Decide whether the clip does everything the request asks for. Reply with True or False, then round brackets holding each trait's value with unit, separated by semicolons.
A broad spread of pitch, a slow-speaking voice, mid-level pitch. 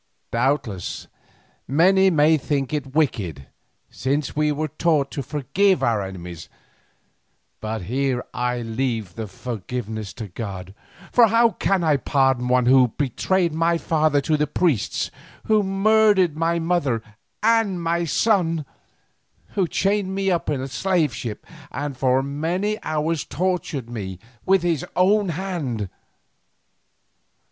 True (6.4 semitones; 130 wpm; 150 Hz)